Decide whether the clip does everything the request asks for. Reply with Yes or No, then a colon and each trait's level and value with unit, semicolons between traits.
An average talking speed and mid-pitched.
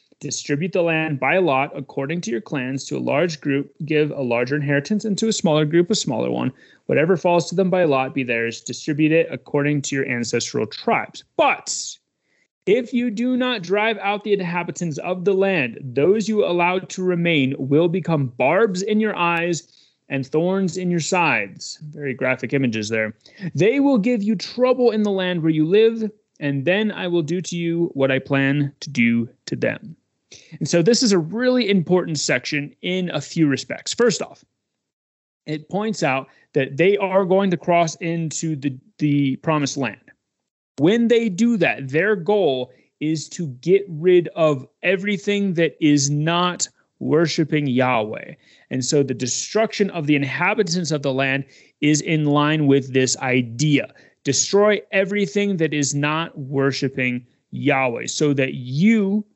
Yes: average, 170 wpm; medium, 160 Hz